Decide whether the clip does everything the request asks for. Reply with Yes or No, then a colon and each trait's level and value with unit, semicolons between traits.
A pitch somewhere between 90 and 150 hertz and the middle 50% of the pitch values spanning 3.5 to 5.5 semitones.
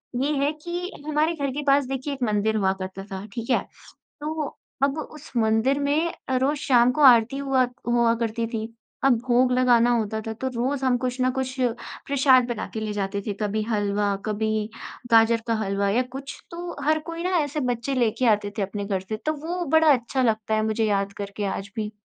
No: high, 240 Hz; average, 4.2 semitones